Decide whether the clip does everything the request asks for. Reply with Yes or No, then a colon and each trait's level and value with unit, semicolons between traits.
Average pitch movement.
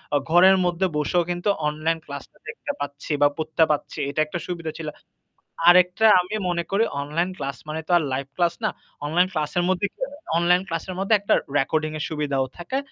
Yes: average, 3.0 semitones